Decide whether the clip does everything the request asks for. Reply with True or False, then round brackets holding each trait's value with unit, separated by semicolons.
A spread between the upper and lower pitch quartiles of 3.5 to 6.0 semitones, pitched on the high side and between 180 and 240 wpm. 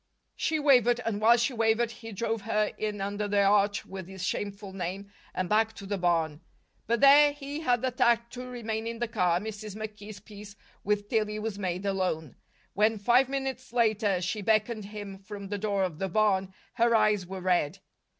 False (2.9 semitones; 210 Hz; 195 wpm)